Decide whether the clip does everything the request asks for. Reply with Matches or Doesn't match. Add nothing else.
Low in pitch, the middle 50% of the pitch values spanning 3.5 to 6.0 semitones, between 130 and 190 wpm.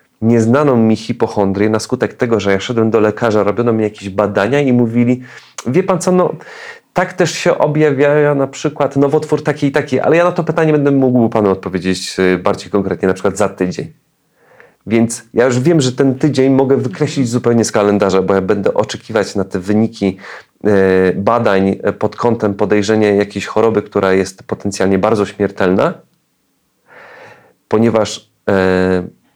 Matches